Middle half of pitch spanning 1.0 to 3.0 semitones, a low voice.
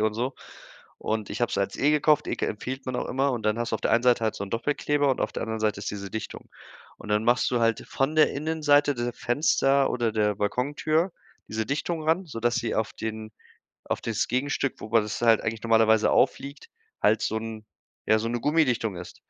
No: average, 4.3 semitones; low, 120 Hz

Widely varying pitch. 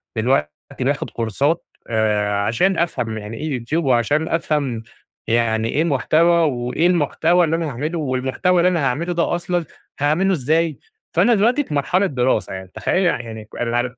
Yes: wide, 6.4 semitones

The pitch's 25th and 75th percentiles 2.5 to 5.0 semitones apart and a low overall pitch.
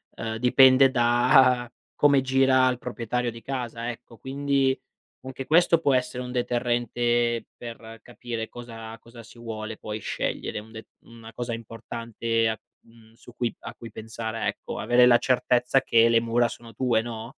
No: narrow, 1.8 semitones; low, 120 Hz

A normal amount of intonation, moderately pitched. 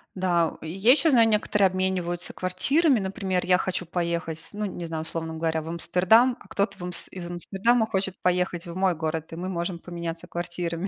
No: narrow, 2.2 semitones; medium, 180 Hz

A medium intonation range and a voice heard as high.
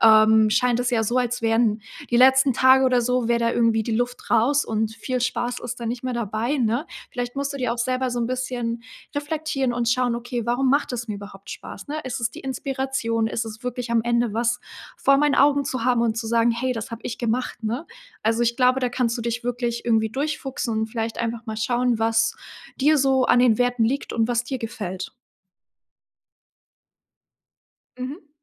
No: narrow, 2.0 semitones; high, 240 Hz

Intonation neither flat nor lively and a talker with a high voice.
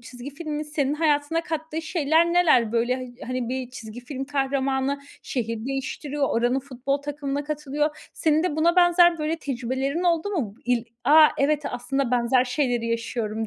Yes: average, 3.6 semitones; very high, 275 Hz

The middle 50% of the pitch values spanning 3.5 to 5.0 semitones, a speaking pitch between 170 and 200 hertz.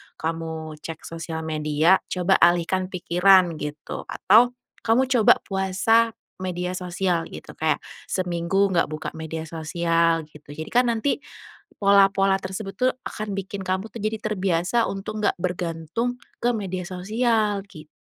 Yes: average, 3.8 semitones; medium, 185 Hz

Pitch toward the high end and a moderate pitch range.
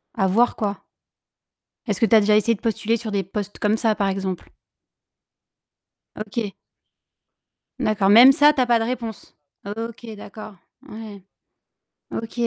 No: high, 215 Hz; narrow, 2.2 semitones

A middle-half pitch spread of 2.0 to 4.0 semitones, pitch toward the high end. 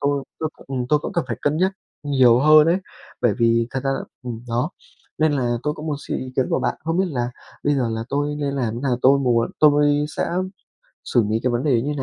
No: average, 3.5 semitones; low, 135 Hz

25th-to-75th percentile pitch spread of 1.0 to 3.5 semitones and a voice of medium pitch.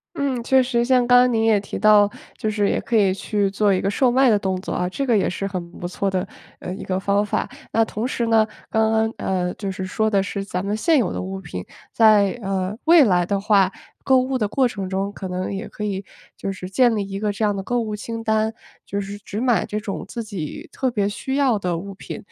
No: average, 2.9 semitones; high, 205 Hz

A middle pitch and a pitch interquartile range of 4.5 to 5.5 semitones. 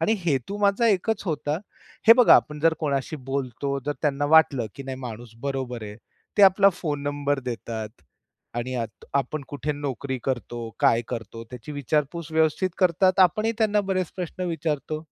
Yes: medium, 145 Hz; average, 4.9 semitones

